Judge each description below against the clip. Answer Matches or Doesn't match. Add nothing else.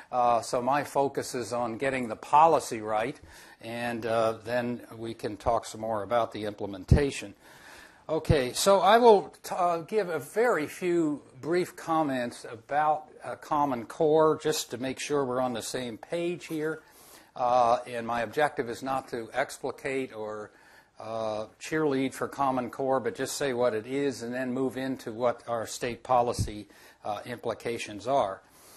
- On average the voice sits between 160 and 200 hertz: Doesn't match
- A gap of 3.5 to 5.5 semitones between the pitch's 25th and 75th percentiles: Matches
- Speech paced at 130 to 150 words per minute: Doesn't match